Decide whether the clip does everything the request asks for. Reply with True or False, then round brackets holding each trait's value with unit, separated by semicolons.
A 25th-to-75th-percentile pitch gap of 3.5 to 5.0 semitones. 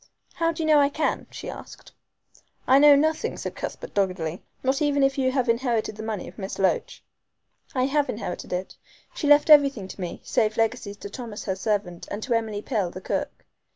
False (5.6 semitones)